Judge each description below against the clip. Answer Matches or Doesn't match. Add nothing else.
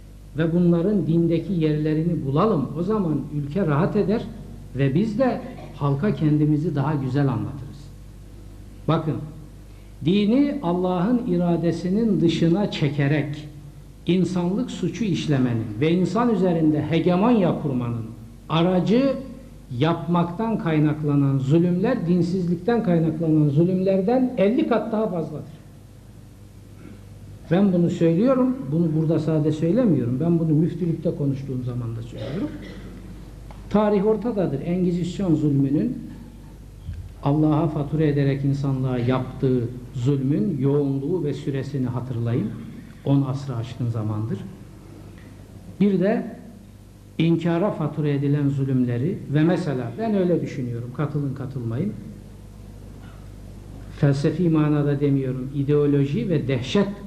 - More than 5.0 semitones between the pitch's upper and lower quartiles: Matches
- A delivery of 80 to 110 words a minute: Matches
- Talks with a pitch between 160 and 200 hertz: Doesn't match